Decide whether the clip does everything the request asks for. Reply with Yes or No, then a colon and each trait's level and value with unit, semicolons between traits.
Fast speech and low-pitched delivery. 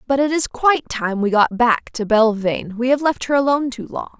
No: fast, 245 wpm; high, 245 Hz